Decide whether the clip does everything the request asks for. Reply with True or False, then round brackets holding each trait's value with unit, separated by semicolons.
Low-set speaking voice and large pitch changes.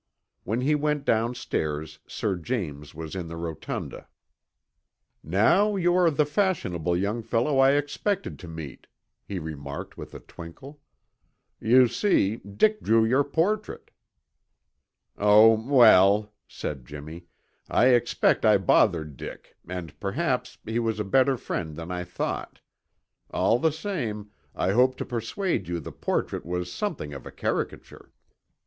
True (110 Hz; 7.9 semitones)